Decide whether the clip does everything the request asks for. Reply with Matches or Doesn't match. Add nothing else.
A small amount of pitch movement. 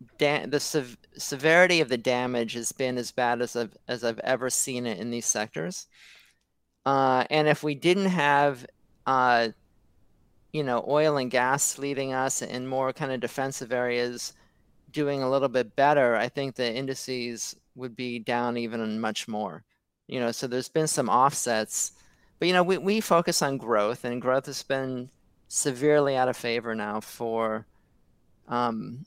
Doesn't match